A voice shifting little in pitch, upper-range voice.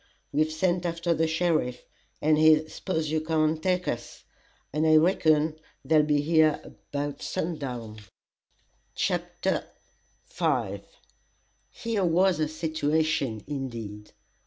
No: narrow, 2.2 semitones; medium, 155 Hz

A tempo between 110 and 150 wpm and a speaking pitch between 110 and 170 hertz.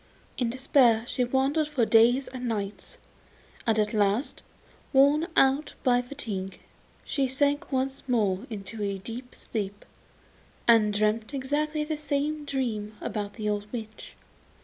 No: average, 140 wpm; high, 245 Hz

